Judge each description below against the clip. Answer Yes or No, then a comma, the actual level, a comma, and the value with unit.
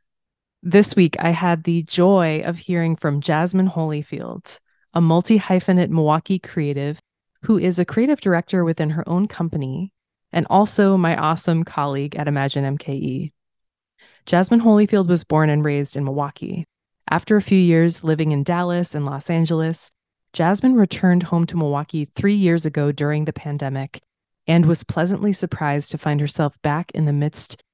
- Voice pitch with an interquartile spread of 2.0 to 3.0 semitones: No, average, 3.4 semitones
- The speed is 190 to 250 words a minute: No, average, 160 wpm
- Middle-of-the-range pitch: Yes, medium, 165 Hz